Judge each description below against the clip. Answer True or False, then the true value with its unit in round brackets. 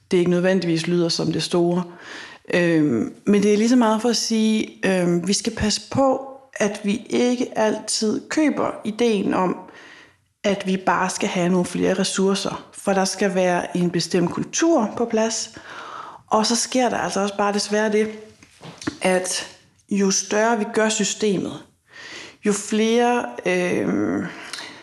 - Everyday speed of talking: True (160 wpm)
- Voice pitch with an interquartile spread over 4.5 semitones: False (3.7 semitones)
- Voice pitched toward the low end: False (210 Hz)